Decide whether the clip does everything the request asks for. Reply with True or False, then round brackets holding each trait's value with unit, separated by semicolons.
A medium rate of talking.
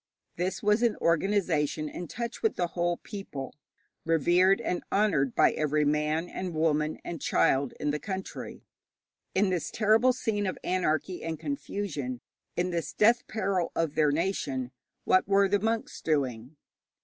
True (150 wpm)